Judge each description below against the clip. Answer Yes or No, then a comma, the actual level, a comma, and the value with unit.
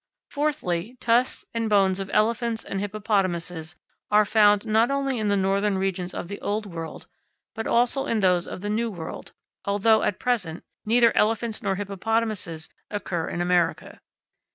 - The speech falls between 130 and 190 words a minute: Yes, average, 155 wpm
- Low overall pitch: No, high, 205 Hz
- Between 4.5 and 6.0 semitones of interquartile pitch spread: No, average, 3.4 semitones